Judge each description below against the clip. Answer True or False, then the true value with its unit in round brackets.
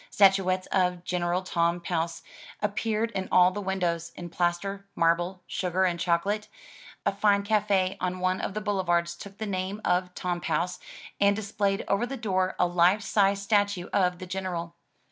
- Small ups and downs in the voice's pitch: True (2.3 semitones)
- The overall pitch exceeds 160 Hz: True (185 Hz)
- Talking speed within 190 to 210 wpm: False (170 wpm)